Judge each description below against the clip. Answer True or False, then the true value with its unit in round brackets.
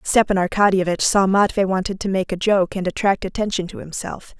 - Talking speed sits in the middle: True (190 wpm)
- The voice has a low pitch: False (190 Hz)